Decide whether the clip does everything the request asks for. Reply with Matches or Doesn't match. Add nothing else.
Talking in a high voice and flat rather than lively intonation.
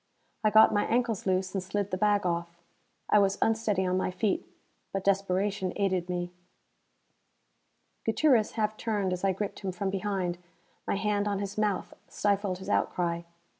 Matches